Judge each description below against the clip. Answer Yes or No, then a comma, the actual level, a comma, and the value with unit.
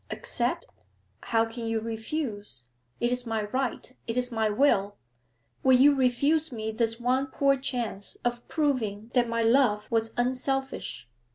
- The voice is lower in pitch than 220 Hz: No, high, 240 Hz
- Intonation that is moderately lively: Yes, average, 3.0 semitones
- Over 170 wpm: No, average, 150 wpm